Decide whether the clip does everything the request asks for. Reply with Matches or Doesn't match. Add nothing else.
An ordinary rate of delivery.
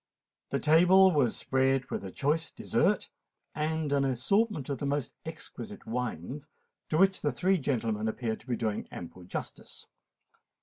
Matches